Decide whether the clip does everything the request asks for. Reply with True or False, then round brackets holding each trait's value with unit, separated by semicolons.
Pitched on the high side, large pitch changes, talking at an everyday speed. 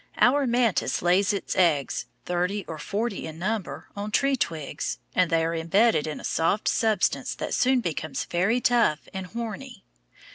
True (195 Hz; 5.7 semitones; 160 wpm)